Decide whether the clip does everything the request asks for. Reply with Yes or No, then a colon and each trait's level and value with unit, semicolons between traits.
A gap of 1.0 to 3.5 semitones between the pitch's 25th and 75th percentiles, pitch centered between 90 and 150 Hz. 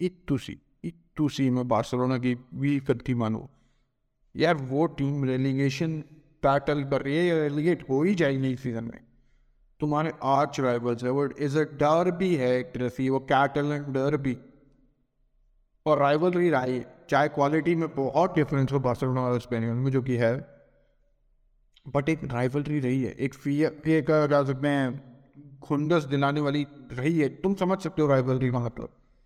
Yes: average, 2.7 semitones; medium, 140 Hz